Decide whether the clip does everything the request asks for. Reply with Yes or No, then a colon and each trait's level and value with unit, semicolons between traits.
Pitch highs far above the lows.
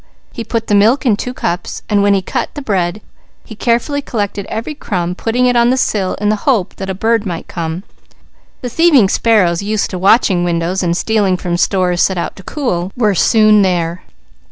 No: average, 4.1 semitones